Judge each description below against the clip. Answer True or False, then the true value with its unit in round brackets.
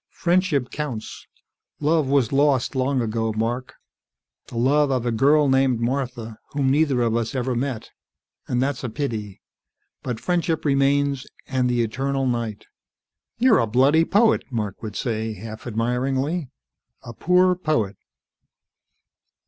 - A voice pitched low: True (130 Hz)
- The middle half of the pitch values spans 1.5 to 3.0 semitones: False (3.6 semitones)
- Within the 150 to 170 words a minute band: False (135 wpm)